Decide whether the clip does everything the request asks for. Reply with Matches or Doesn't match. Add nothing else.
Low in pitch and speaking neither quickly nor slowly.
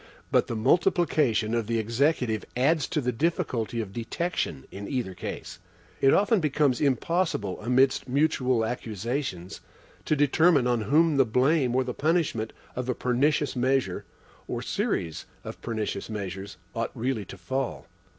Matches